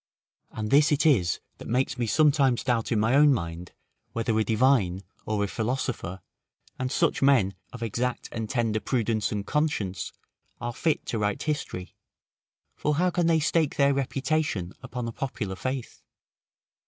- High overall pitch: No, low, 120 Hz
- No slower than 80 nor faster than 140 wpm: No, average, 160 wpm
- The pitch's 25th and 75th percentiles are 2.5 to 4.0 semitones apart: No, average, 4.7 semitones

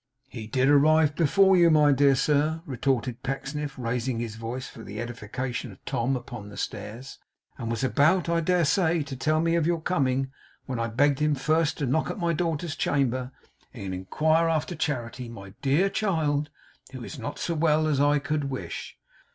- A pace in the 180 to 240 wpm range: Yes, average, 185 wpm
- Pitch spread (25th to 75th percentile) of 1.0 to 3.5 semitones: No, average, 4.1 semitones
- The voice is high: No, medium, 140 Hz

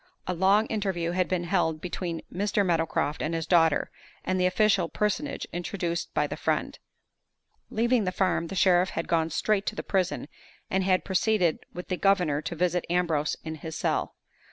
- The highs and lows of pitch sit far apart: No, average, 2.7 semitones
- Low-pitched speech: No, medium, 180 Hz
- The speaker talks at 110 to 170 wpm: No, average, 180 wpm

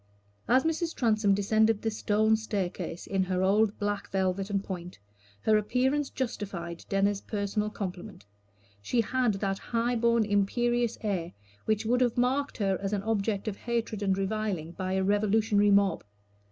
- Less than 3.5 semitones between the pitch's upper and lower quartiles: Yes, narrow, 2.6 semitones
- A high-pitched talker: Yes, high, 205 Hz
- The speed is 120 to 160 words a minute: Yes, average, 155 wpm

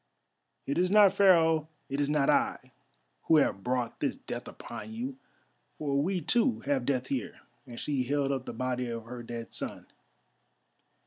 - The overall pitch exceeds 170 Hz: No, medium, 140 Hz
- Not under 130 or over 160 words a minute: No, average, 170 wpm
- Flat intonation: No, average, 5.2 semitones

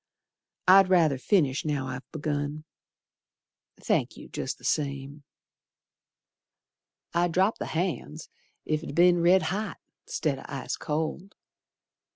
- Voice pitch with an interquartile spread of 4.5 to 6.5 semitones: No, average, 3.8 semitones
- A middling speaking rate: No, slow, 120 wpm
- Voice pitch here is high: No, medium, 155 Hz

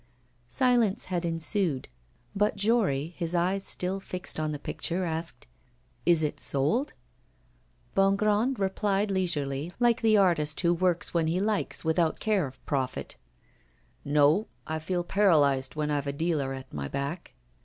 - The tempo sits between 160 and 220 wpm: No, average, 145 wpm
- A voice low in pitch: No, medium, 170 Hz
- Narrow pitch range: No, average, 4.8 semitones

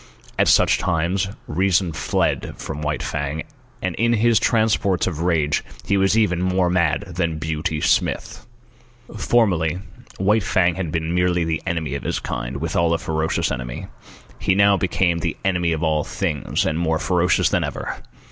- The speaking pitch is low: Yes, very low, 85 Hz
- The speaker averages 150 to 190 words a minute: Yes, average, 165 wpm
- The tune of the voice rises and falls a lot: No, average, 3.1 semitones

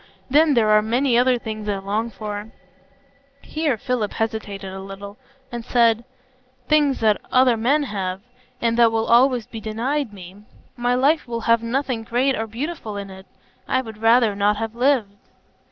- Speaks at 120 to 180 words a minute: Yes, average, 165 wpm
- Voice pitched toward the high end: Yes, high, 230 Hz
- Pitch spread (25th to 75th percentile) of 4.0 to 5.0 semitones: No, average, 3.3 semitones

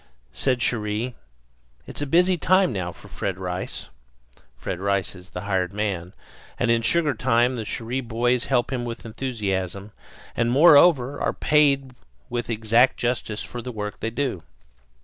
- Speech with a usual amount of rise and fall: Yes, average, 4.1 semitones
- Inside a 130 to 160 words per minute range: Yes, average, 155 wpm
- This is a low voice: Yes, low, 115 Hz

